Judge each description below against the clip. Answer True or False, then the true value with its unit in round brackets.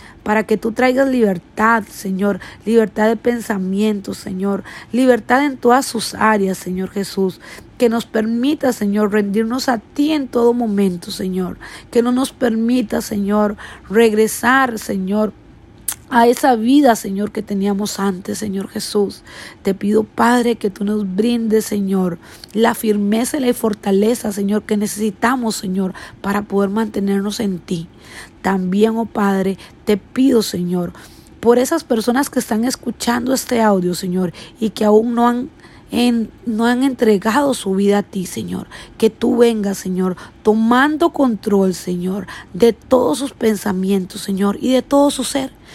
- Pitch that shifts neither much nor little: True (3.3 semitones)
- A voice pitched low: False (215 Hz)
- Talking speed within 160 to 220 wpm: False (145 wpm)